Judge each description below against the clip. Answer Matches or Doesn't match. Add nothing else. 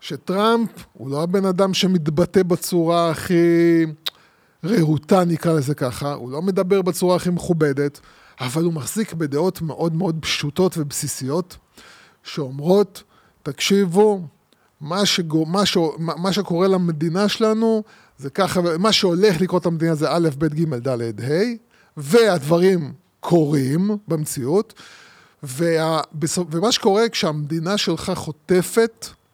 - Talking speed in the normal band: Matches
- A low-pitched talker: Doesn't match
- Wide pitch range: Doesn't match